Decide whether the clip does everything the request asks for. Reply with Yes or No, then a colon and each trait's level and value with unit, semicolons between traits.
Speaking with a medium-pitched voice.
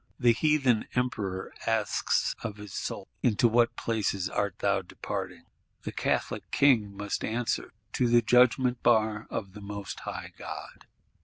No: low, 110 Hz